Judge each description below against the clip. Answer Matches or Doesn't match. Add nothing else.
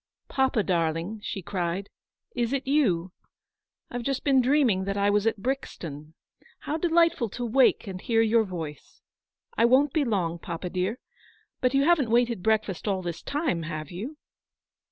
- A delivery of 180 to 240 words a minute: Doesn't match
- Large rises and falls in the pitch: Matches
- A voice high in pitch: Matches